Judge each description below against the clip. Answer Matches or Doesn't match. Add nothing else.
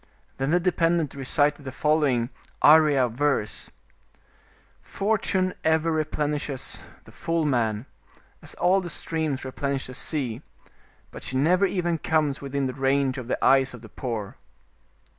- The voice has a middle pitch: Matches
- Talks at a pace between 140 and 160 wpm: Matches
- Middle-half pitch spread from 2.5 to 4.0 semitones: Matches